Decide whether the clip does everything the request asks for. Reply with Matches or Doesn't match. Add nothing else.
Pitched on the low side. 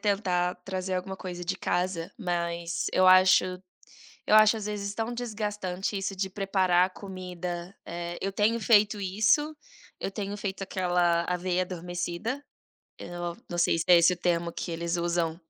Doesn't match